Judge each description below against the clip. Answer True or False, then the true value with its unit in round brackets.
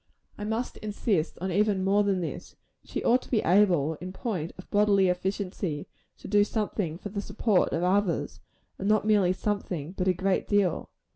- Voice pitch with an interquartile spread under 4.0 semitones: True (2.5 semitones)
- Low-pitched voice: False (195 Hz)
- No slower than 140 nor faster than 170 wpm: False (185 wpm)